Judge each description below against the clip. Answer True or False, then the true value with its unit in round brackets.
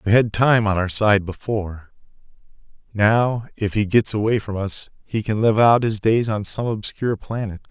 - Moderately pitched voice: False (105 Hz)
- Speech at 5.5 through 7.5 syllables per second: False (4.8 syllables/s)